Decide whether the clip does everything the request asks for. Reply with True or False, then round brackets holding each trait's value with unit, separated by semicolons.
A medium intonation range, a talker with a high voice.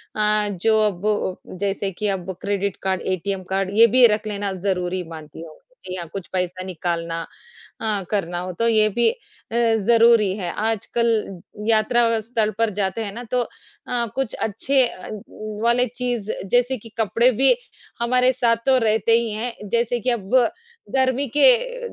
True (3.7 semitones; 220 Hz)